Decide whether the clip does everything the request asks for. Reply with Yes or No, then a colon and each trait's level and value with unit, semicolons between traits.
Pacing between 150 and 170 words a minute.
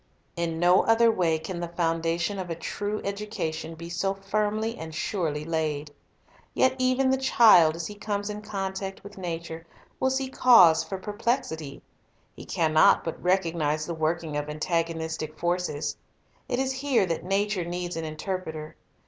Yes: average, 165 wpm